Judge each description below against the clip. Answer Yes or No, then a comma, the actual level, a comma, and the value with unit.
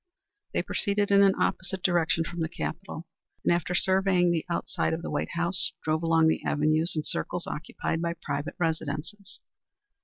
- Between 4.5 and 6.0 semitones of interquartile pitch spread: No, narrow, 2.5 semitones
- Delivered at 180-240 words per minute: No, average, 165 wpm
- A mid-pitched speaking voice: Yes, medium, 170 Hz